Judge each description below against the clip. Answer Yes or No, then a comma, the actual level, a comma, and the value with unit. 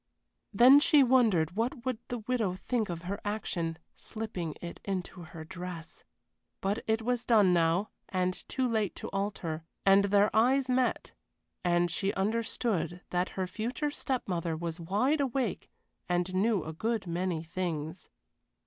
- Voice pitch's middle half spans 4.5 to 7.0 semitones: Yes, average, 4.8 semitones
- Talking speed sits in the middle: Yes, average, 150 wpm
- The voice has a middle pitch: No, high, 195 Hz